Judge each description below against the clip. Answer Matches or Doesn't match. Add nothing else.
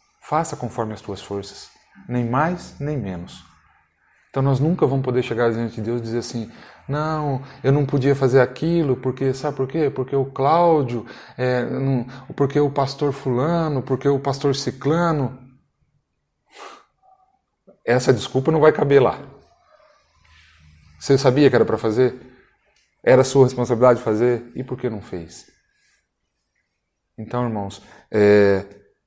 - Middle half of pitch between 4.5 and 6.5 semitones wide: Doesn't match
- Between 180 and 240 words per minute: Doesn't match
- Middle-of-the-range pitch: Doesn't match